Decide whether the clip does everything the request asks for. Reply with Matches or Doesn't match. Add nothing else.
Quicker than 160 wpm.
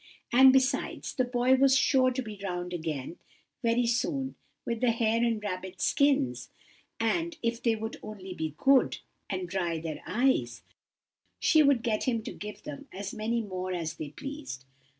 Matches